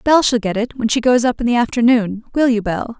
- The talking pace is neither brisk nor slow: No, fast, 280 wpm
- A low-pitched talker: No, high, 235 Hz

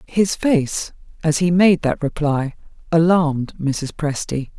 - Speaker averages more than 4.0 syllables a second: No, 3.8 syllables/s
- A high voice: No, medium, 160 Hz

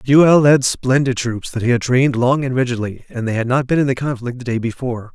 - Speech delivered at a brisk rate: Yes, fast, 255 wpm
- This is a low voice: Yes, low, 125 Hz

